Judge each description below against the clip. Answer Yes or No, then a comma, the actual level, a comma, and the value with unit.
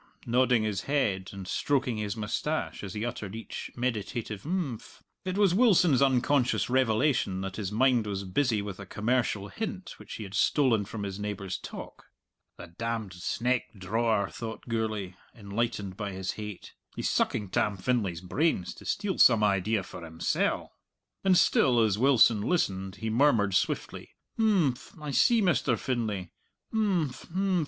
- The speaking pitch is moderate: No, low, 110 Hz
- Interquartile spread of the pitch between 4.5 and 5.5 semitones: Yes, average, 5.1 semitones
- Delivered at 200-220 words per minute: No, average, 150 wpm